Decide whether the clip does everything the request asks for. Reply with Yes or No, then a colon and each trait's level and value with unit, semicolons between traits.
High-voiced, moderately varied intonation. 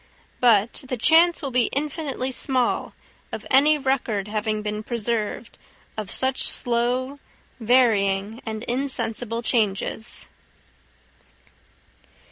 Yes: high, 240 Hz; average, 3.5 semitones